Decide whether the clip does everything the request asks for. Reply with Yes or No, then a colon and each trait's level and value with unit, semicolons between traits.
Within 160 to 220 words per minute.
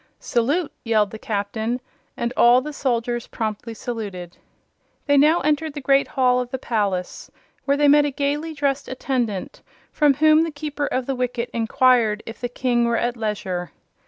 Yes: average, 170 wpm